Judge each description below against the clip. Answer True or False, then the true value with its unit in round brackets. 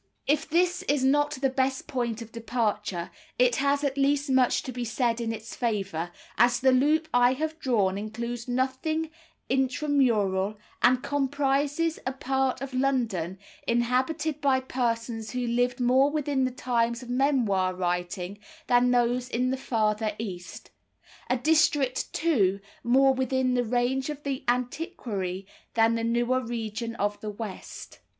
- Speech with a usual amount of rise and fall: True (3.0 semitones)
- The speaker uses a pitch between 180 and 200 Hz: False (250 Hz)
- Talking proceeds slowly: False (150 wpm)